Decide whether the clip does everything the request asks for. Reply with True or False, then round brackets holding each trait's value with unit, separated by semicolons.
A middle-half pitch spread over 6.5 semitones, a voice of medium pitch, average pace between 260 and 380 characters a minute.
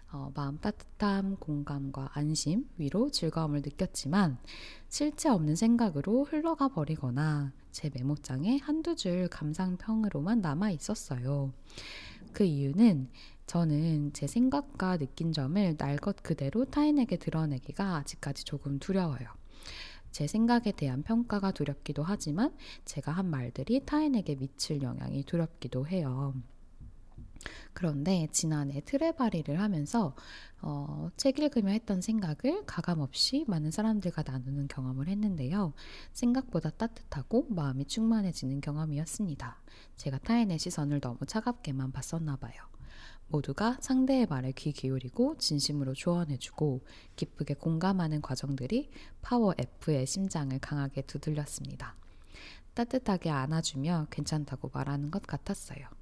True (6.9 semitones; 160 Hz; 305 characters per minute)